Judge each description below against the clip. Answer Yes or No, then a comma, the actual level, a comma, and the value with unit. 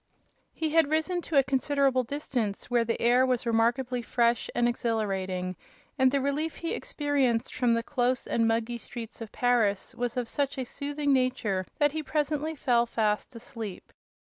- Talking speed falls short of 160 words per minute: No, average, 170 wpm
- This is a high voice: Yes, high, 245 Hz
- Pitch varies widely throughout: No, average, 3.5 semitones